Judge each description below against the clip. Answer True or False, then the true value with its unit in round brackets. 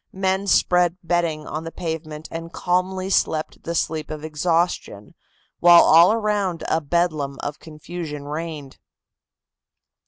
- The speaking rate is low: True (125 wpm)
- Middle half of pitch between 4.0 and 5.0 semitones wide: False (2.5 semitones)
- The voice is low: False (165 Hz)